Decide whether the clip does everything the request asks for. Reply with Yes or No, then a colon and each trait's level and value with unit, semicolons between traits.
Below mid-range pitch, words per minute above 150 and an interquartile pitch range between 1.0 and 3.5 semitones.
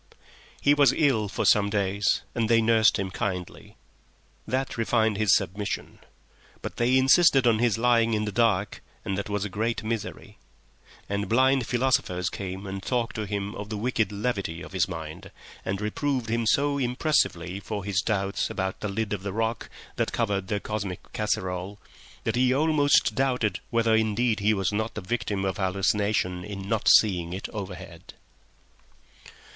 Yes: low, 105 Hz; average, 165 wpm; average, 3.2 semitones